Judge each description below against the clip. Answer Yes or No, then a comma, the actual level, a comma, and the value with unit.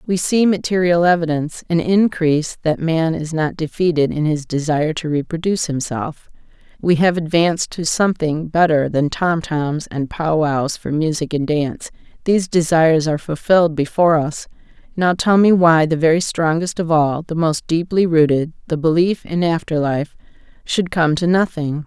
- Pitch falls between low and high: Yes, medium, 160 Hz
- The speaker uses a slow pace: No, average, 165 wpm